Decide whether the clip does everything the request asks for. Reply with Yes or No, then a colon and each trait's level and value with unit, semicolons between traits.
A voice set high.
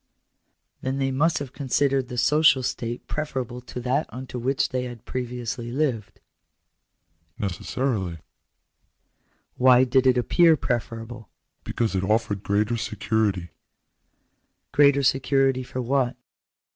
No: low, 125 Hz